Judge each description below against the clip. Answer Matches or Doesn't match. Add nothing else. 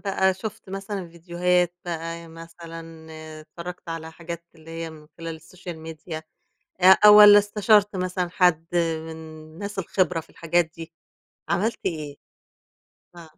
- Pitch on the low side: Doesn't match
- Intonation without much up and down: Matches